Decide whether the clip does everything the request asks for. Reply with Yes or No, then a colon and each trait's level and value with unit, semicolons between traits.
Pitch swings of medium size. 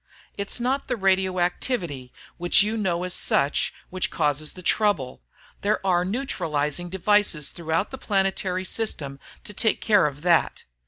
Yes: average, 4.5 semitones